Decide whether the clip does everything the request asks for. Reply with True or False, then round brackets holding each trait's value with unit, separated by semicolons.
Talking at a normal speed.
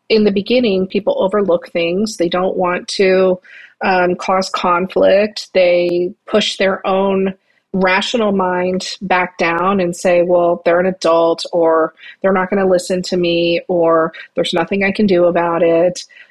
True (160 wpm)